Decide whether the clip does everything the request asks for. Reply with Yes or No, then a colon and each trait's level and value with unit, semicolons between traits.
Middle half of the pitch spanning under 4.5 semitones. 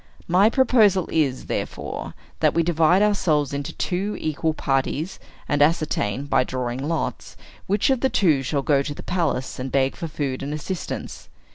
No: average, 4.8 semitones